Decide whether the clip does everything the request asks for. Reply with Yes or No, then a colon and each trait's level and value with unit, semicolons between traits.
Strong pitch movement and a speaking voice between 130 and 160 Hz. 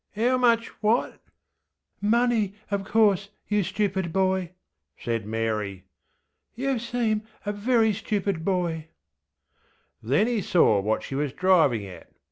No: wide, 8.2 semitones; high, 190 Hz